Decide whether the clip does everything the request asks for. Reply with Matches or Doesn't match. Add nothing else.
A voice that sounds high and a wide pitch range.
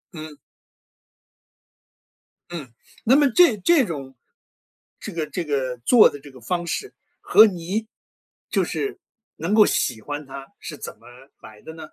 Doesn't match